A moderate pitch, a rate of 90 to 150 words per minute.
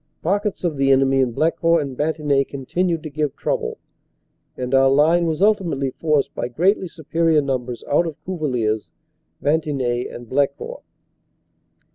Yes: medium, 150 Hz; average, 145 wpm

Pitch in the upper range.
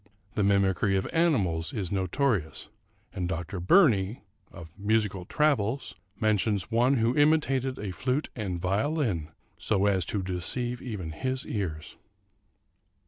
No: low, 105 Hz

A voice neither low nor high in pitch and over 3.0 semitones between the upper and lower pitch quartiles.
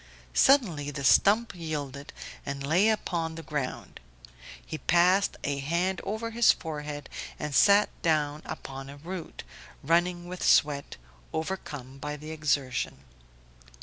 Yes: medium, 155 Hz; average, 4.1 semitones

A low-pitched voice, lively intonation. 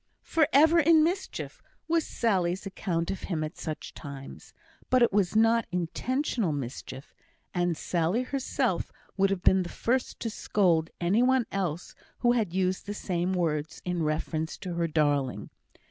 No: medium, 185 Hz; wide, 6.0 semitones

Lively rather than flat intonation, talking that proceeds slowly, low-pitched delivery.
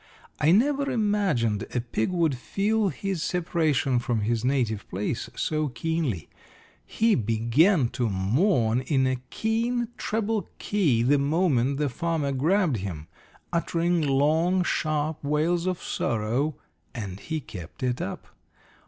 No: wide, 6.9 semitones; slow, 130 wpm; medium, 150 Hz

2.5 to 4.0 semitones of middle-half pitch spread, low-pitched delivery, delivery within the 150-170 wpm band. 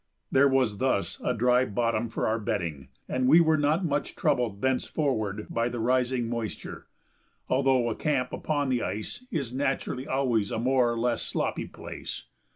Yes: average, 2.8 semitones; low, 125 Hz; average, 165 wpm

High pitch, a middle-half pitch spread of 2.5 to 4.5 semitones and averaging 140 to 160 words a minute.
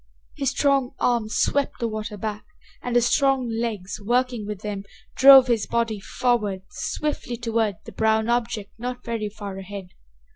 Yes: high, 230 Hz; average, 2.8 semitones; average, 155 wpm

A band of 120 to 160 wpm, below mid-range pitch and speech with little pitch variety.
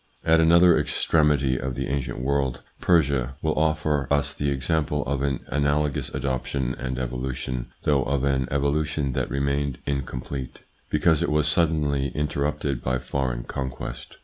Yes: average, 145 wpm; very low, 70 Hz; narrow, 2.3 semitones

